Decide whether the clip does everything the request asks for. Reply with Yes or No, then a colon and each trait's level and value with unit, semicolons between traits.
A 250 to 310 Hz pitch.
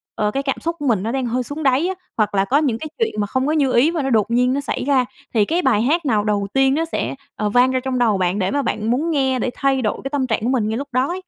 Yes: very high, 260 Hz